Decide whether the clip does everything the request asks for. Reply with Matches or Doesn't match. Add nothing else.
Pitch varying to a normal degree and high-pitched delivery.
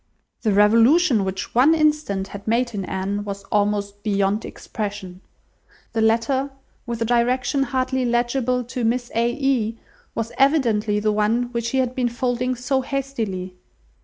Matches